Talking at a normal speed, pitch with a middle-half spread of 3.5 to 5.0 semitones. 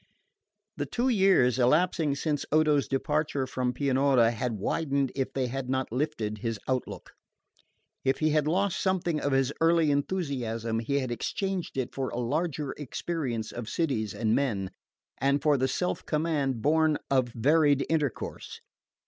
Yes: average, 150 wpm; average, 3.8 semitones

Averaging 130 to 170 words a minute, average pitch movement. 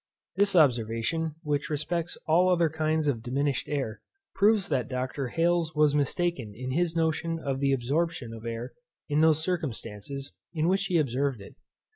Yes: average, 160 wpm; average, 4.4 semitones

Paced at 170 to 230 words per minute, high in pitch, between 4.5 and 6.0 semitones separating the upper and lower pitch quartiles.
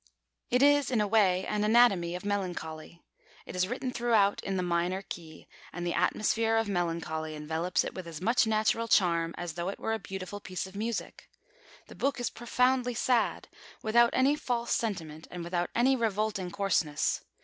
Yes: average, 180 wpm; high, 200 Hz; average, 4.8 semitones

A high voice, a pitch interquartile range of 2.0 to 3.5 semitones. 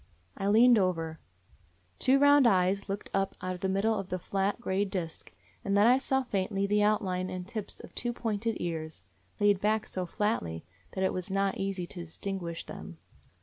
Yes: high, 195 Hz; narrow, 2.6 semitones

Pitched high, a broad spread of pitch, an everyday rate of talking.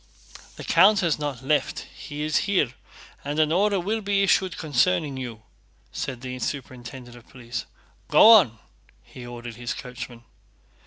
No: medium, 140 Hz; wide, 6.3 semitones; average, 150 wpm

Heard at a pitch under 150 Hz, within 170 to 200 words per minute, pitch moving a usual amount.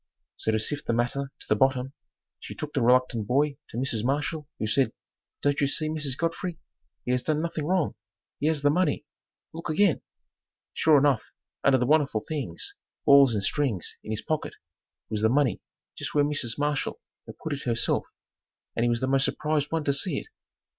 Yes: medium, 140 Hz; average, 195 wpm; average, 3.5 semitones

